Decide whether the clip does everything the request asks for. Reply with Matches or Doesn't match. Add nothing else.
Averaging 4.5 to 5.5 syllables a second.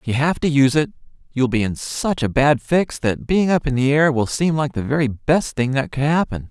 Matches